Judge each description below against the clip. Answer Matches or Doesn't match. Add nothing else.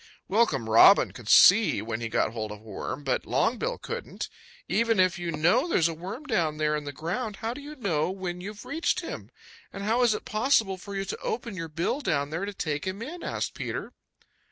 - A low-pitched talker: Doesn't match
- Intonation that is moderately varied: Doesn't match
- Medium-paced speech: Doesn't match